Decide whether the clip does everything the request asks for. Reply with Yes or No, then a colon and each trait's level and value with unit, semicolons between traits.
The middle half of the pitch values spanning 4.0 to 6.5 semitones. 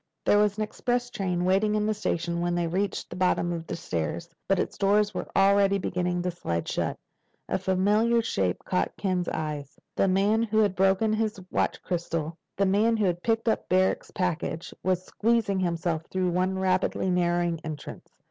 No: average, 3.0 semitones